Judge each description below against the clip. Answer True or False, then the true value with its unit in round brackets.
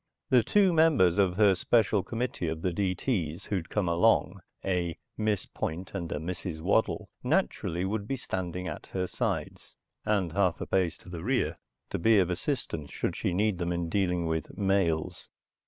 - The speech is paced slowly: False (175 wpm)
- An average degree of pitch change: True (3.3 semitones)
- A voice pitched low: True (95 Hz)